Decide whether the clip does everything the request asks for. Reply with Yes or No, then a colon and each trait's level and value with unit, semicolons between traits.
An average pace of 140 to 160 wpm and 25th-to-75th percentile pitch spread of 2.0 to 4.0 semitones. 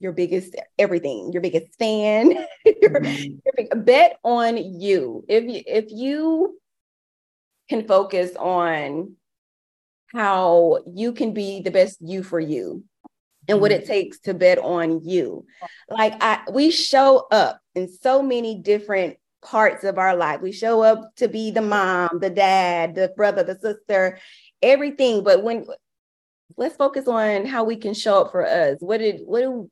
No: average, 155 wpm; average, 4.7 semitones